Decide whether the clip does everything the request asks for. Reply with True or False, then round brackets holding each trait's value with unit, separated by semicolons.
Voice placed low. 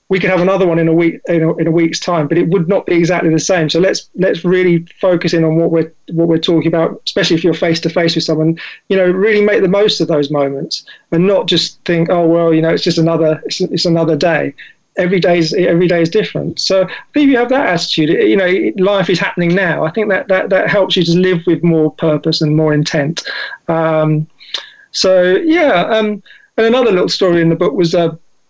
False (170 Hz)